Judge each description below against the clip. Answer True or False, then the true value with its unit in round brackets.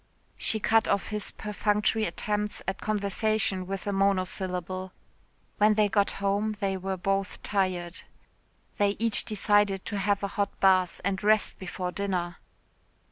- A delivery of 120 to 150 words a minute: True (140 wpm)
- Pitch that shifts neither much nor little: False (1.8 semitones)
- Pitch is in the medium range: False (200 Hz)